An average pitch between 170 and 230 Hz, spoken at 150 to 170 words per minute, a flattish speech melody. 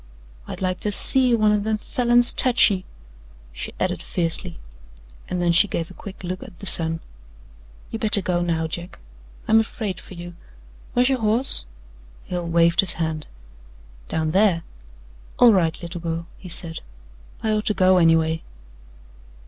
No: medium, 185 Hz; average, 160 wpm; average, 4.3 semitones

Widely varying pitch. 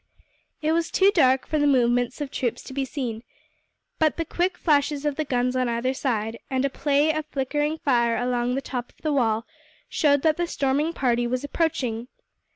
No: average, 3.6 semitones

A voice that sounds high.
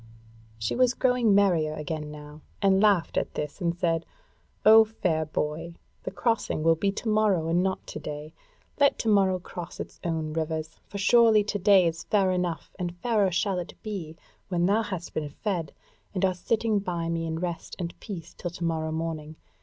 No: medium, 175 Hz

